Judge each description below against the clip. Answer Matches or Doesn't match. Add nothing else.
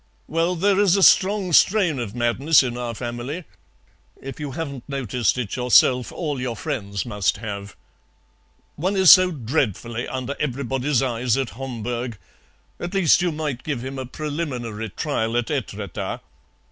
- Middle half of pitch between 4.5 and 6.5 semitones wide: Matches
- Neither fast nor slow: Matches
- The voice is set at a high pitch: Doesn't match